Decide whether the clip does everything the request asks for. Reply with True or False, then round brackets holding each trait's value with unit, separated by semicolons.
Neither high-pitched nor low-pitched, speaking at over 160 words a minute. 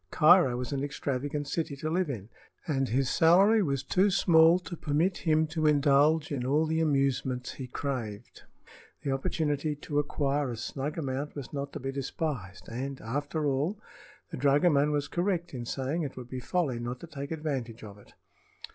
True (145 Hz; 180 wpm)